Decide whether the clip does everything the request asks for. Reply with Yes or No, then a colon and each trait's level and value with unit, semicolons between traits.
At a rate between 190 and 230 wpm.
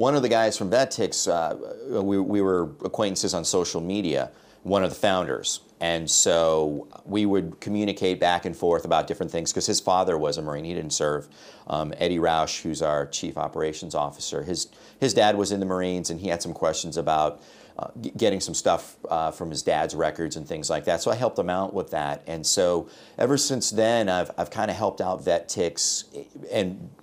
Yes: fast, 205 wpm